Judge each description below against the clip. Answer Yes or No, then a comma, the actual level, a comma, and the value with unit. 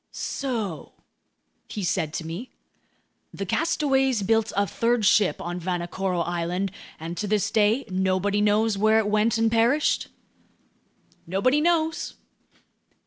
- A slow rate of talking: Yes, slow, 125 wpm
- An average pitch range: Yes, average, 3.8 semitones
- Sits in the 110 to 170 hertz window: No, high, 210 Hz